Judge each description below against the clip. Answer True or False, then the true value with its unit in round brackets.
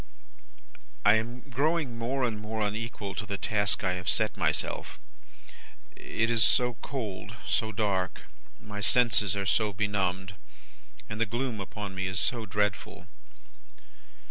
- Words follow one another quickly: False (140 wpm)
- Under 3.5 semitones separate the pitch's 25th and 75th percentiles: True (2.8 semitones)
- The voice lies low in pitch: True (105 Hz)